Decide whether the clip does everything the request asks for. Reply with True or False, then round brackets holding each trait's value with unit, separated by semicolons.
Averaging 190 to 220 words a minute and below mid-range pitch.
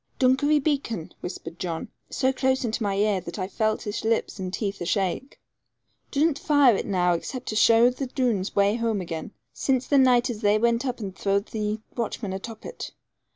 False (195 wpm; 220 Hz)